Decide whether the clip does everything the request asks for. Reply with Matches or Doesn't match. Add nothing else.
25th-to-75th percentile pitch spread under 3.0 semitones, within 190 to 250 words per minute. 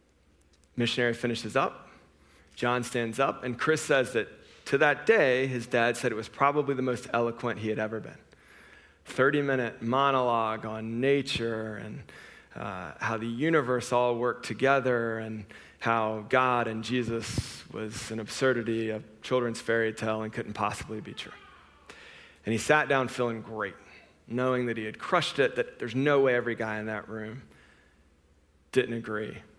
Doesn't match